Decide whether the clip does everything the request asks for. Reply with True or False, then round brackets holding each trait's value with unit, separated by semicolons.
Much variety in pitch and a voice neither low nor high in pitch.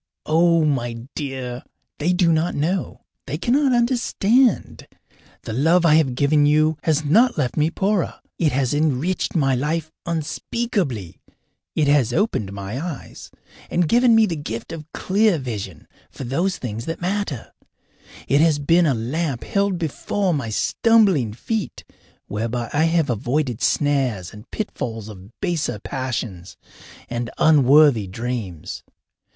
True (6.0 semitones; 150 Hz)